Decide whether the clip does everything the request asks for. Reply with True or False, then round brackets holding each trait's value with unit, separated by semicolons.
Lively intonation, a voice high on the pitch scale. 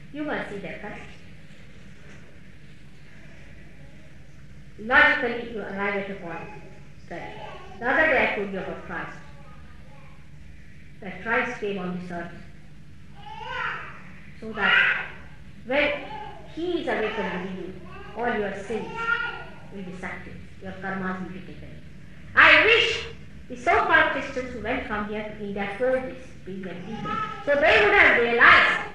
True (7.8 semitones; 210 Hz)